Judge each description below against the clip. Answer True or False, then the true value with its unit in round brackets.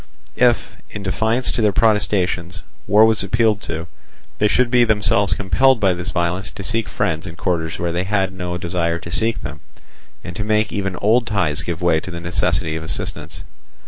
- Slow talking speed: False (190 wpm)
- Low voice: True (95 Hz)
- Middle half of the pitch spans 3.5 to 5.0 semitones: True (3.8 semitones)